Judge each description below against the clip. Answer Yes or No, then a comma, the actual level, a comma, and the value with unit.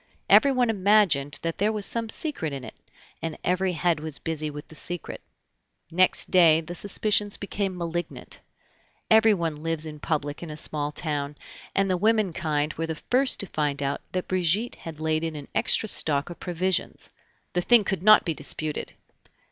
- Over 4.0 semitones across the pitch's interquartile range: Yes, average, 4.4 semitones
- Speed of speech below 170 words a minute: No, average, 175 wpm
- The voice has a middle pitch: Yes, medium, 170 Hz